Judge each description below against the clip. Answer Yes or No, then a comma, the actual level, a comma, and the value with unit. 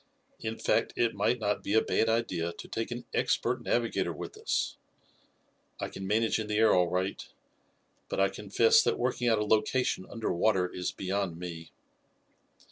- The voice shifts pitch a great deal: No, average, 3.4 semitones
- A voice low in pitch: Yes, low, 105 Hz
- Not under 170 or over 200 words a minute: Yes, average, 175 wpm